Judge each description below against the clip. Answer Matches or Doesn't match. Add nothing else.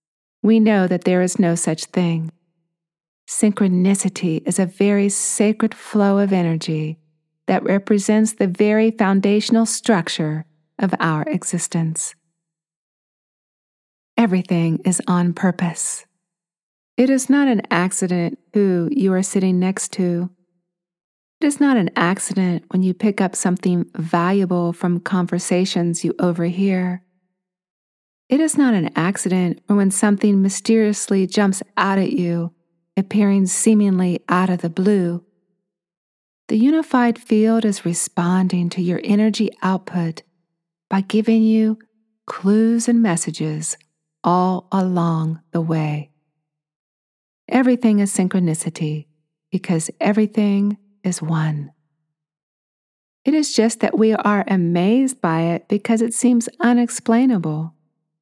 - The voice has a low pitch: Doesn't match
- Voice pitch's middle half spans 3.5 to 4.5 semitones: Matches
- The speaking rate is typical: Doesn't match